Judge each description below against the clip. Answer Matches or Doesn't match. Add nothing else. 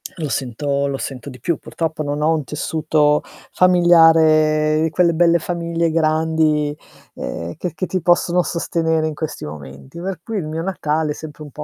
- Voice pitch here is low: Doesn't match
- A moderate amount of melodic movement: Doesn't match